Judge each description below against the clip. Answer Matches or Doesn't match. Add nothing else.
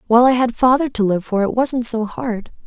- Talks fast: Matches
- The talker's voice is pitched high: Matches